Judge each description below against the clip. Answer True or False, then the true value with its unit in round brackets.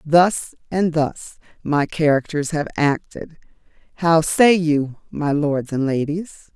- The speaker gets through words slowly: True (130 wpm)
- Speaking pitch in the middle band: True (155 Hz)